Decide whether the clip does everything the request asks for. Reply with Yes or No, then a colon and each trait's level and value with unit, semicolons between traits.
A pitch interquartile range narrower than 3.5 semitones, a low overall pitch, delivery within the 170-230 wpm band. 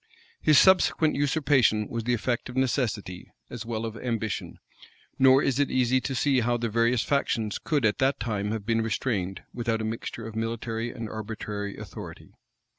Yes: average, 2.9 semitones; low, 115 Hz; average, 180 wpm